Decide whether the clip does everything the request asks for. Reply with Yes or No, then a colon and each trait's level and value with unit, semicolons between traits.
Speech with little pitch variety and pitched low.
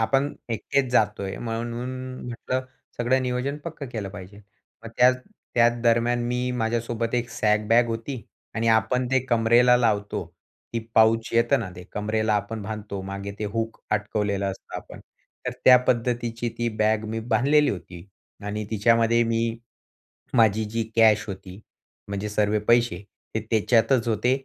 Yes: narrow, 2.3 semitones; low, 115 Hz